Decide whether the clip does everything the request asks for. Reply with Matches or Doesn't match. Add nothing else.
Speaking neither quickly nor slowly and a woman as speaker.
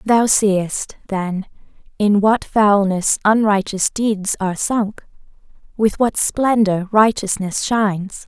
Doesn't match